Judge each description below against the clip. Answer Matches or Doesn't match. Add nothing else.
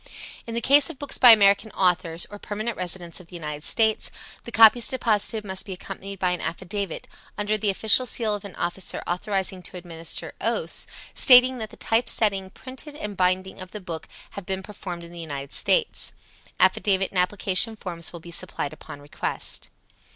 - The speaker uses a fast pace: Doesn't match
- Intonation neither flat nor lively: Matches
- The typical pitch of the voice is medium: Doesn't match